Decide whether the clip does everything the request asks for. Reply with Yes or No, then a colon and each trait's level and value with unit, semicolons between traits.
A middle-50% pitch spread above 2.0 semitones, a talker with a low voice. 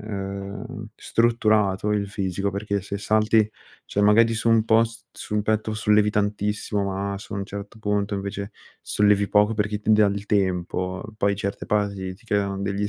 No: narrow, 1.3 semitones; low, 105 Hz